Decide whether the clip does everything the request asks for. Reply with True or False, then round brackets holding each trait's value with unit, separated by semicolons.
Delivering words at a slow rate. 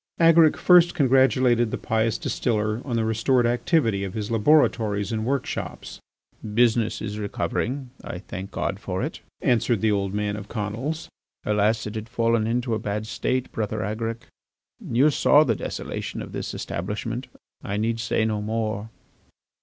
False (155 wpm)